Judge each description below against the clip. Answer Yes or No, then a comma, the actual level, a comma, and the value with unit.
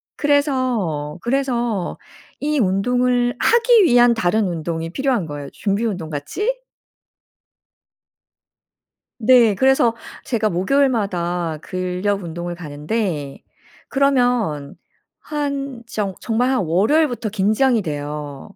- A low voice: No, high, 220 Hz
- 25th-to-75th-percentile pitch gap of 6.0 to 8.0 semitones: Yes, wide, 6.9 semitones